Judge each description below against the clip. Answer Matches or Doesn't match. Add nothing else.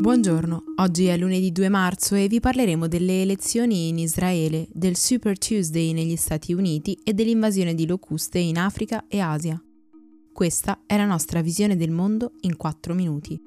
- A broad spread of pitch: Doesn't match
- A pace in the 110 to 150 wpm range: Doesn't match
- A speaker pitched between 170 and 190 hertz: Matches